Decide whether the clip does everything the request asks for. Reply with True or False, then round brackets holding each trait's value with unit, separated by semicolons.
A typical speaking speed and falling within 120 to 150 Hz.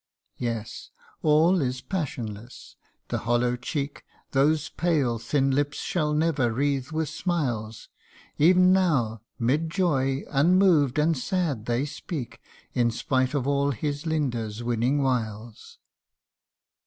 False (115 wpm; 140 Hz)